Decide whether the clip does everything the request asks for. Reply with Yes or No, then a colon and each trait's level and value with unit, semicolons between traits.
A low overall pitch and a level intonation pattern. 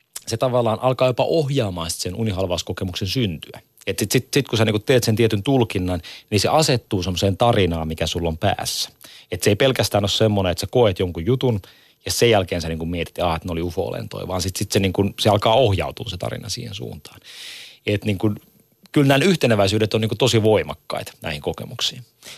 No: low, 105 Hz; average, 4.9 semitones